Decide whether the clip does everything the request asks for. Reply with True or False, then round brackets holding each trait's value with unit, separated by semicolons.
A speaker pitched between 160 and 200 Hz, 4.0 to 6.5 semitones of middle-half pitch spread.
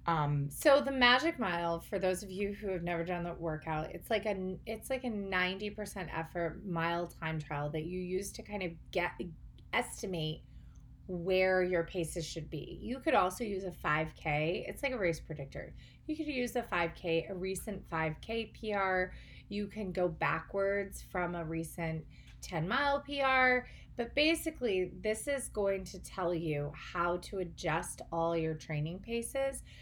True (185 Hz; 4.3 semitones)